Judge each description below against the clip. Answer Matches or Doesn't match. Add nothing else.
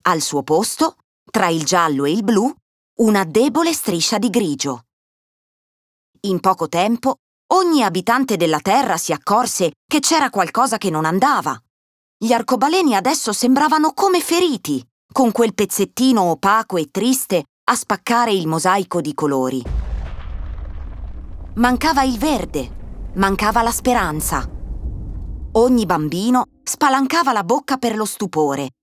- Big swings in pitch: Matches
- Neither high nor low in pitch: Doesn't match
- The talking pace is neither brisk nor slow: Matches